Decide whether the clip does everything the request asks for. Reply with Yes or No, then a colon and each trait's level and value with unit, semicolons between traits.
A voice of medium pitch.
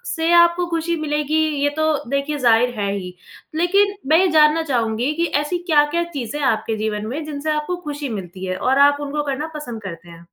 No: very high, 290 Hz